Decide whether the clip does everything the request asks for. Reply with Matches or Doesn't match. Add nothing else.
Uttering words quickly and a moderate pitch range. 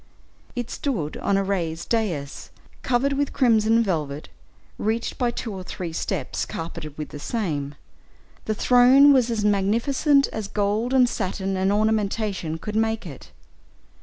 Doesn't match